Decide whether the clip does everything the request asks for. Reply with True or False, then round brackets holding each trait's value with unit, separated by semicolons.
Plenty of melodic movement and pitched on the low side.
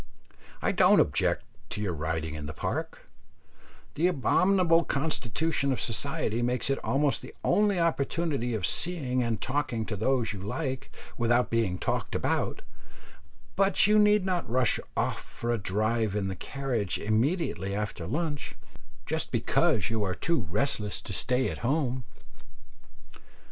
True (6.7 semitones; 125 Hz)